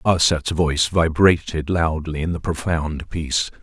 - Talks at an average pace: No, slow, 130 wpm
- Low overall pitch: Yes, very low, 80 Hz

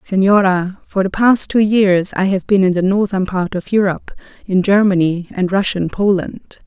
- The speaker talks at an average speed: Yes, average, 180 wpm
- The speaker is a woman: Yes, female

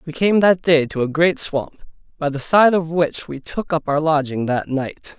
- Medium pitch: Yes, medium, 155 Hz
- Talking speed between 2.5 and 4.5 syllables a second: Yes, 4.4 syllables/s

